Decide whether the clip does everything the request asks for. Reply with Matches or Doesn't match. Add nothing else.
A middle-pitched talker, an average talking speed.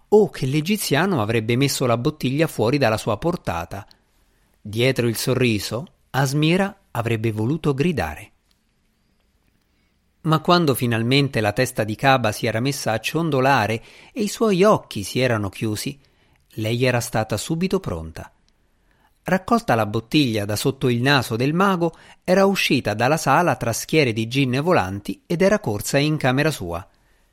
Doesn't match